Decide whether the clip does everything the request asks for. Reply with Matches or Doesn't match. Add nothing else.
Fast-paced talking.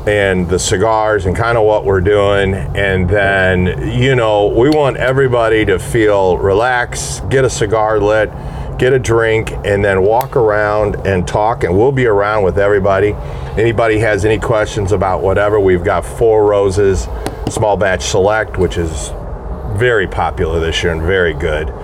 Doesn't match